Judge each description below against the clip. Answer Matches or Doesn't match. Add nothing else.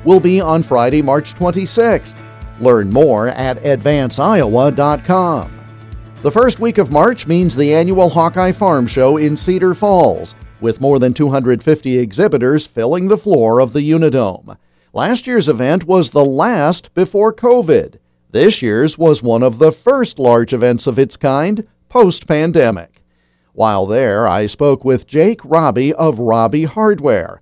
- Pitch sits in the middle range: Matches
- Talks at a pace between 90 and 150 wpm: Matches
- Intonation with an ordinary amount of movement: Doesn't match